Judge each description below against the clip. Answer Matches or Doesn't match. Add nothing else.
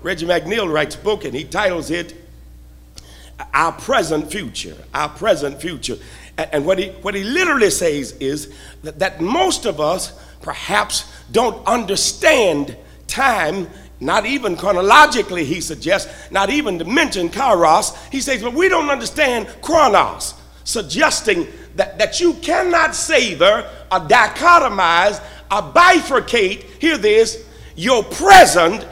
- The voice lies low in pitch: Doesn't match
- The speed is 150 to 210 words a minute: Doesn't match